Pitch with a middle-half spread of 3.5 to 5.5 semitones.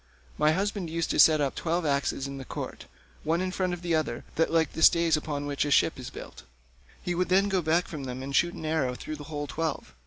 No: average, 3.1 semitones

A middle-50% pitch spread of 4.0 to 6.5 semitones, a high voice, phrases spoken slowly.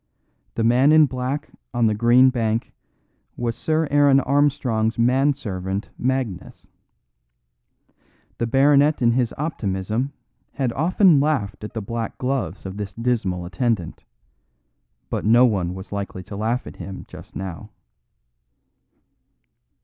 No: average, 4.8 semitones; low, 120 Hz; slow, 125 wpm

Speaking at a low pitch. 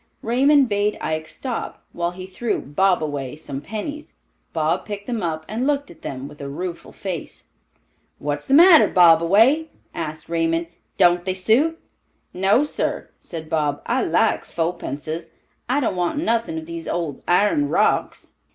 No: medium, 180 Hz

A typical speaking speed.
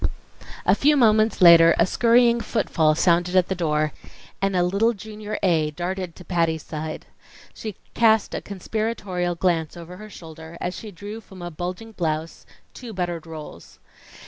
Yes: average, 160 wpm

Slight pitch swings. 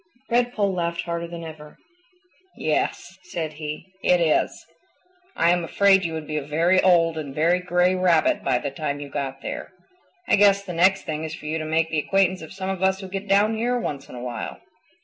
No: average, 3.5 semitones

